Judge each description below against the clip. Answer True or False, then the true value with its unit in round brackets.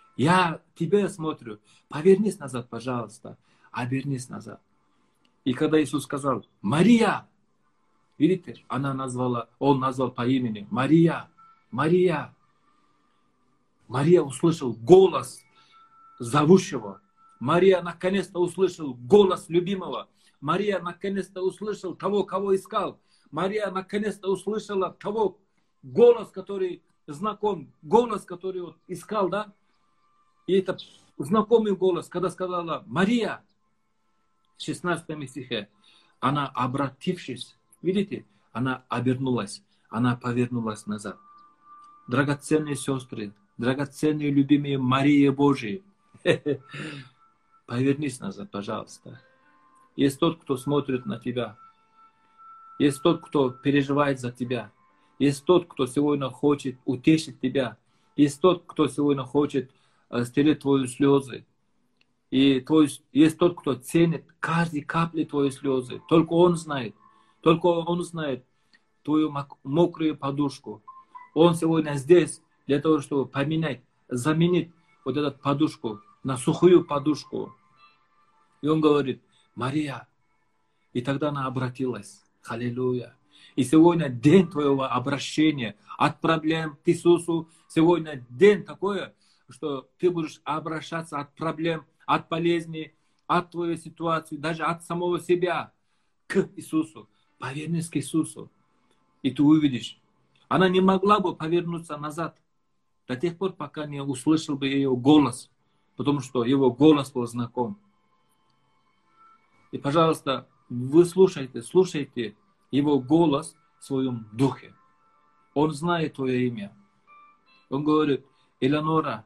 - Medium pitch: True (150 Hz)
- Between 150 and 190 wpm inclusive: False (110 wpm)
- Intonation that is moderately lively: True (4.6 semitones)